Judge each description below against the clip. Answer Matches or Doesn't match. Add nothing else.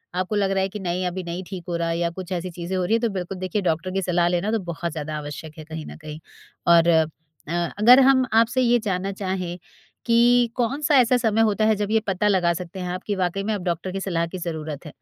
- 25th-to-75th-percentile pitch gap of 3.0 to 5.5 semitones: Matches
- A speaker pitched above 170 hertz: Matches